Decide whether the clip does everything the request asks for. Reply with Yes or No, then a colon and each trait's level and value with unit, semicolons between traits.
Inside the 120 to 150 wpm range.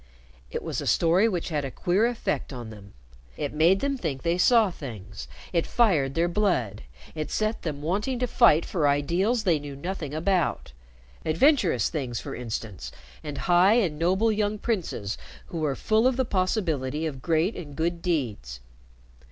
No: average, 170 wpm